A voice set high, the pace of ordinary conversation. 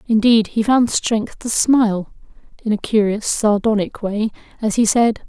Yes: high, 215 Hz; average, 160 wpm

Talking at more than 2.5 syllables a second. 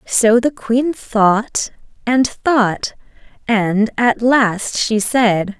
No: 2.4 syllables/s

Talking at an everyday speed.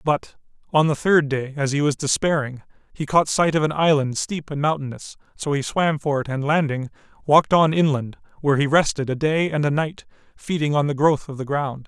No: fast, 215 wpm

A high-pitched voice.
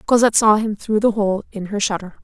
Yes: high, 210 Hz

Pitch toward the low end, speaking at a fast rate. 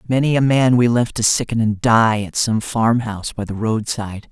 Yes: low, 115 Hz; fast, 210 wpm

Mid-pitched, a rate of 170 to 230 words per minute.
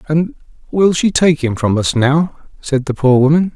Yes: medium, 150 Hz; average, 200 wpm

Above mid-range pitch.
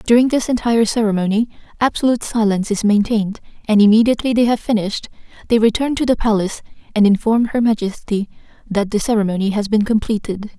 Yes: high, 220 Hz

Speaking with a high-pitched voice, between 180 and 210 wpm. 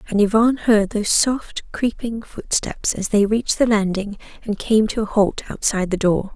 Yes: high, 210 Hz; average, 190 wpm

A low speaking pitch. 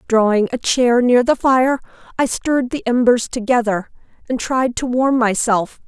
No: high, 245 Hz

